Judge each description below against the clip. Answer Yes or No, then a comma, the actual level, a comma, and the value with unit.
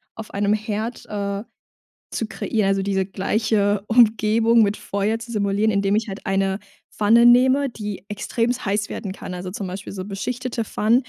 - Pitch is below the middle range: No, high, 210 Hz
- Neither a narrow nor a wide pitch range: No, narrow, 2.3 semitones